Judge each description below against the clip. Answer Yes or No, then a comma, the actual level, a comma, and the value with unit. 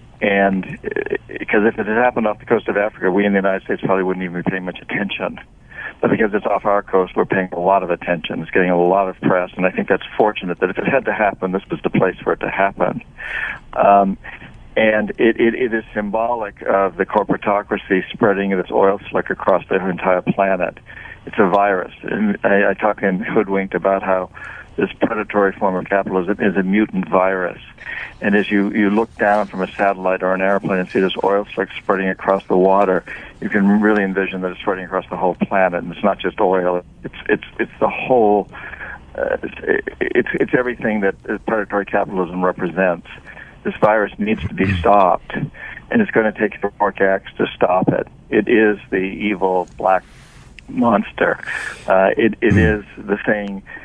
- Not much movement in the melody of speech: Yes, narrow, 1.9 semitones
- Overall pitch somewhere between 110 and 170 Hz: No, low, 100 Hz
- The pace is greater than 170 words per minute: Yes, average, 200 wpm